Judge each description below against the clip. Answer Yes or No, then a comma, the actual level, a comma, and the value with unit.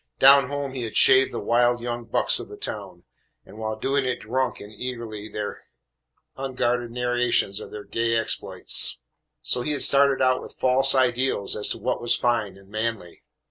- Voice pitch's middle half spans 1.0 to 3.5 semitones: Yes, average, 3.0 semitones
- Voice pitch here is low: Yes, low, 120 Hz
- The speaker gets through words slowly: No, average, 180 wpm